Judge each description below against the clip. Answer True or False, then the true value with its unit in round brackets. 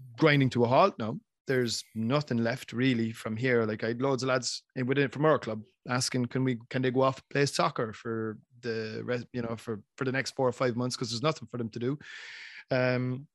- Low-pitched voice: True (125 Hz)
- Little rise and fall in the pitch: True (2.3 semitones)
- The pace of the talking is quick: True (235 wpm)